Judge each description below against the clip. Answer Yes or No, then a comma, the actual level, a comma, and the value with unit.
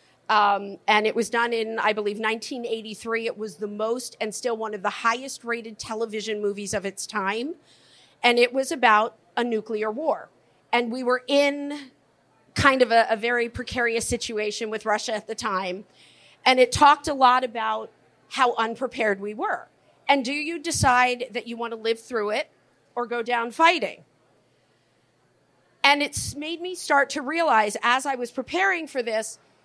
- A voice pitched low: No, high, 235 Hz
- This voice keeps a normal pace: Yes, average, 175 wpm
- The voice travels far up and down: No, average, 3.2 semitones